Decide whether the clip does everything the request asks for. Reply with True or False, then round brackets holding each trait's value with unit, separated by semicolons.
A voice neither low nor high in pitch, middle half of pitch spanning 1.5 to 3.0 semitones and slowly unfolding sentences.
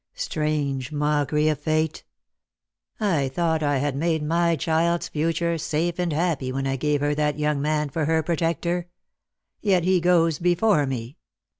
False (155 Hz; 2.6 semitones; 155 wpm)